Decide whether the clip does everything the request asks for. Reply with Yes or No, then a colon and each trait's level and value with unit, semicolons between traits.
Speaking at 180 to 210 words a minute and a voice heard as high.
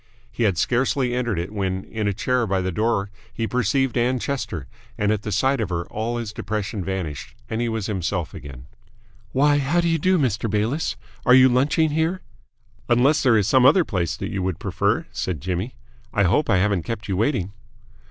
No: average, 200 wpm; low, 110 Hz